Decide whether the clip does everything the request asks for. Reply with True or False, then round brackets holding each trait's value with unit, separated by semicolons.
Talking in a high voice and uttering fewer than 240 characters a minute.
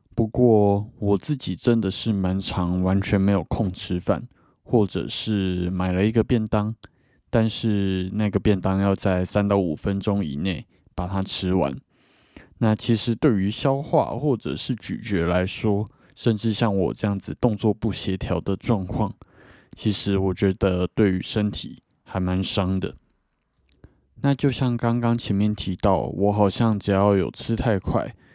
False (100 Hz; 220 characters per minute)